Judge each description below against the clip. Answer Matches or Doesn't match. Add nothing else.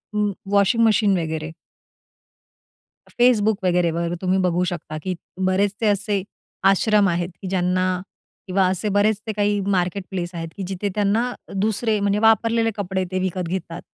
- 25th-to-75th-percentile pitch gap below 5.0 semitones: Matches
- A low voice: Doesn't match